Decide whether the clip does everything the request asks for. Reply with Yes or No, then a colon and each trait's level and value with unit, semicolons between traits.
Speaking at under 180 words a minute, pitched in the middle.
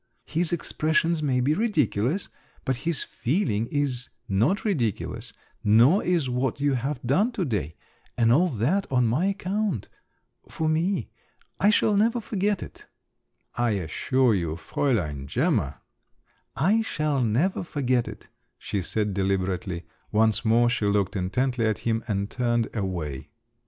No: average, 140 wpm; low, 125 Hz